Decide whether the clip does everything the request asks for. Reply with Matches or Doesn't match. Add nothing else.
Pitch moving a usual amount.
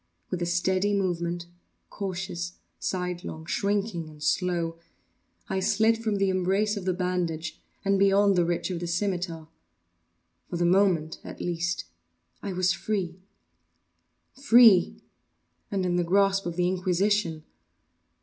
Doesn't match